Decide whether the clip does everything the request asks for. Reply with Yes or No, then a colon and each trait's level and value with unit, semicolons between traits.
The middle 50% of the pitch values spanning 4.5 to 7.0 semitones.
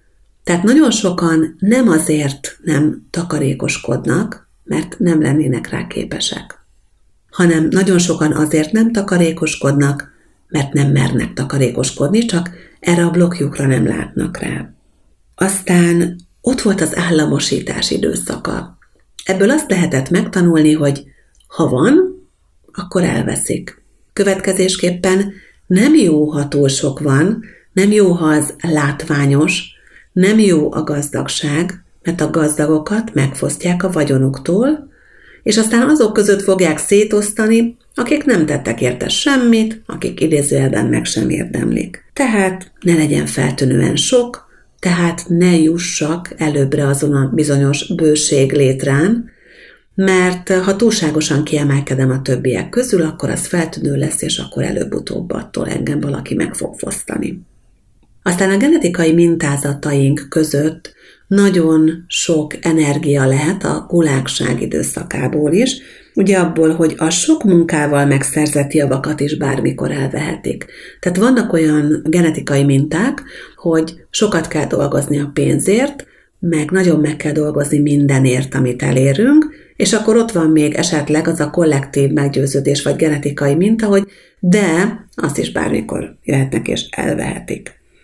Yes: average, 4.8 semitones